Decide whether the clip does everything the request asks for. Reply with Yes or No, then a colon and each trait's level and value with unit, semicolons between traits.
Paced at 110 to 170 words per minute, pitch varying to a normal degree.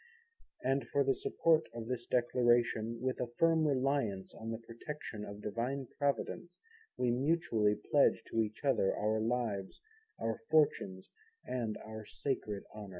Yes: average, 140 wpm; average, 3.9 semitones